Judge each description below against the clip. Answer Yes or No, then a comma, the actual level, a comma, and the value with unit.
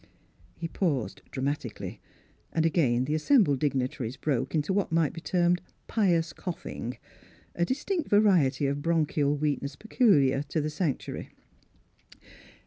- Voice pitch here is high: No, medium, 155 Hz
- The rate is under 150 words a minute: Yes, slow, 135 wpm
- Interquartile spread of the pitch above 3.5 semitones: Yes, average, 4.0 semitones